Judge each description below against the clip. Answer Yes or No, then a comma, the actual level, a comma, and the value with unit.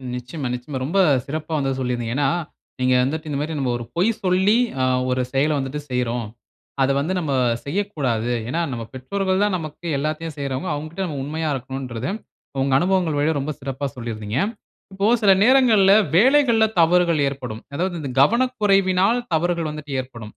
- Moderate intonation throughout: No, wide, 5.9 semitones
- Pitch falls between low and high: Yes, medium, 150 Hz